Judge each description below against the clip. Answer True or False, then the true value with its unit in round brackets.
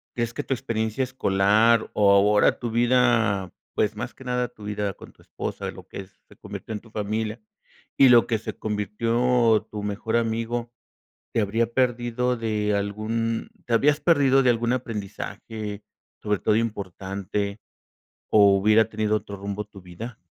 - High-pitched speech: False (110 Hz)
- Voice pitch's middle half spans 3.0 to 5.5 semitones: False (2.4 semitones)